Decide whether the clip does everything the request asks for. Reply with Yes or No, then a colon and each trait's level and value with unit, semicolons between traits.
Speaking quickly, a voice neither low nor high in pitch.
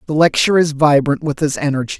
Yes: fast, 210 wpm; medium, 150 Hz